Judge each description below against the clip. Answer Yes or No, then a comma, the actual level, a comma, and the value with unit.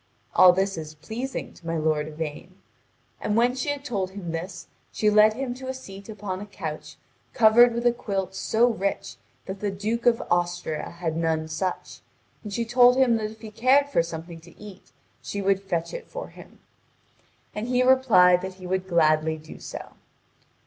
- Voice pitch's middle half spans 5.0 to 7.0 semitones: Yes, wide, 5.4 semitones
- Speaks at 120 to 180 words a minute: No, average, 190 wpm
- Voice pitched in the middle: No, high, 195 Hz